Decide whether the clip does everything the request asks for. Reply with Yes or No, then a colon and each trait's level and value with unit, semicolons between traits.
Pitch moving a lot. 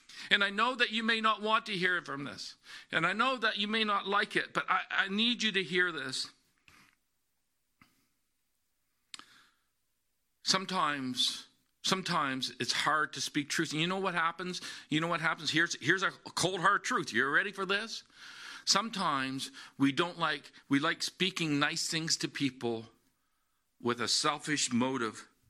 Yes: wide, 6.0 semitones